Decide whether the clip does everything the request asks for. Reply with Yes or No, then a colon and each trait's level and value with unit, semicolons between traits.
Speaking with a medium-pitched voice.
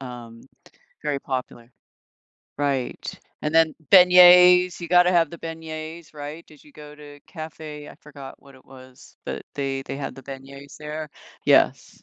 Yes: medium, 150 Hz